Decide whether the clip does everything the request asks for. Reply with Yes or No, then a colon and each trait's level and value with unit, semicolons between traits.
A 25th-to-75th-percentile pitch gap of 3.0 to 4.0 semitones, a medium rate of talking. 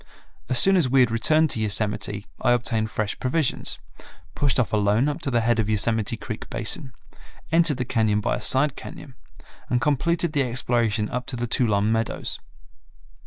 Yes: average, 3.7 semitones; average, 175 wpm